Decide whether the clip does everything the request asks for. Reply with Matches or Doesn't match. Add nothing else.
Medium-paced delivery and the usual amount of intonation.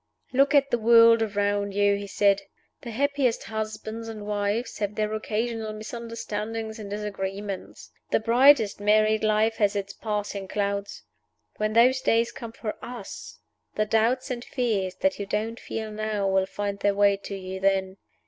Doesn't match